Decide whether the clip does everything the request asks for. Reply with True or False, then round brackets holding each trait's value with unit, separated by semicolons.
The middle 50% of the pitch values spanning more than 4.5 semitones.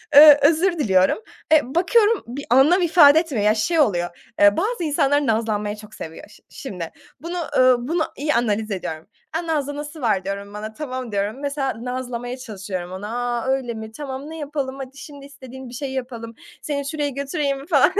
True (5.1 semitones)